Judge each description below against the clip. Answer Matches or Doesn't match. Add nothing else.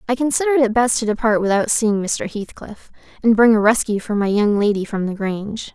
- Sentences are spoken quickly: Matches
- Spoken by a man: Doesn't match